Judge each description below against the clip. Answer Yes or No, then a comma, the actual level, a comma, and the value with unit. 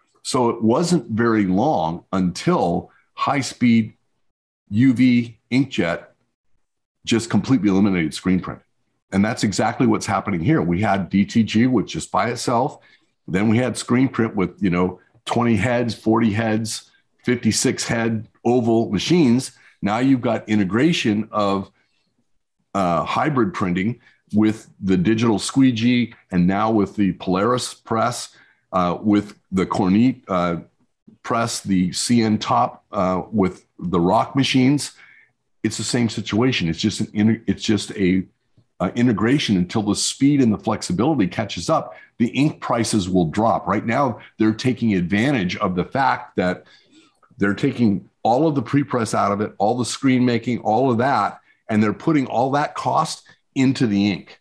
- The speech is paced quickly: No, average, 150 wpm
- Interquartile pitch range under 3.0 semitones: No, average, 3.5 semitones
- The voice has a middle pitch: No, low, 110 Hz